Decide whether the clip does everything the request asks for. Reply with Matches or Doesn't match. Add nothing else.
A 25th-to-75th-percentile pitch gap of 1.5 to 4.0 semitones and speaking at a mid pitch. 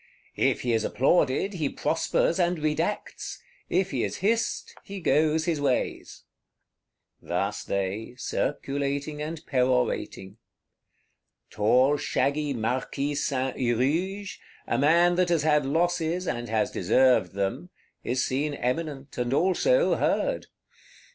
Doesn't match